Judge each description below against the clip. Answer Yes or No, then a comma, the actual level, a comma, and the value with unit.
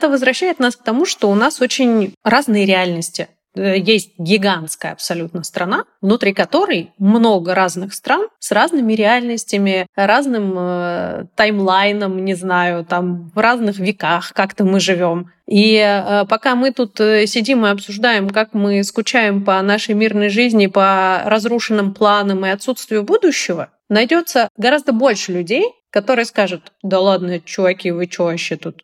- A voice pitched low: No, high, 205 Hz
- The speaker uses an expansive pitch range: No, average, 3.5 semitones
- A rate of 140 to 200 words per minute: Yes, average, 145 wpm